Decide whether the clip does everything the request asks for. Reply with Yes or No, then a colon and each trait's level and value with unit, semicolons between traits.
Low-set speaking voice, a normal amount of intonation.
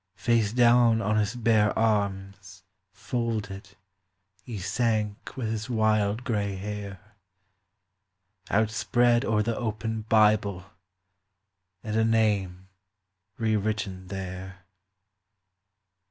No: low, 105 Hz; narrow, 2.1 semitones